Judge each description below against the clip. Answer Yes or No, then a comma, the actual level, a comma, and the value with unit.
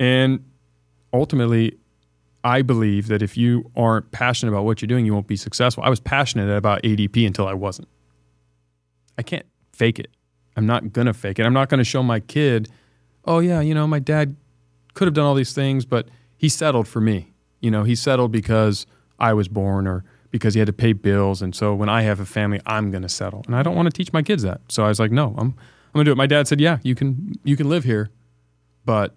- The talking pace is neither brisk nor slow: No, fast, 240 wpm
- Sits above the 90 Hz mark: Yes, low, 110 Hz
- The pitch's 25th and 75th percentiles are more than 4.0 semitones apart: Yes, average, 4.7 semitones